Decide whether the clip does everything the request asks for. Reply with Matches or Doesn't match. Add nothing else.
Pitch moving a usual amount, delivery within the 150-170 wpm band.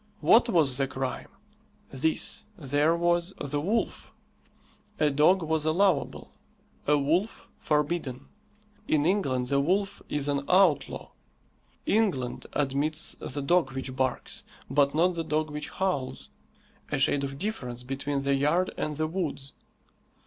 Doesn't match